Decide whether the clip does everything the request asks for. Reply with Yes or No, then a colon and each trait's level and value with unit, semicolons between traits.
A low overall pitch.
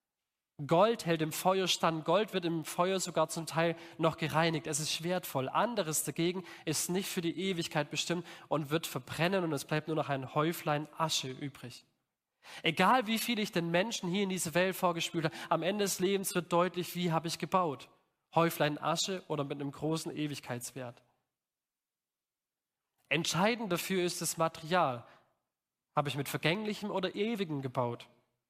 No: medium, 165 Hz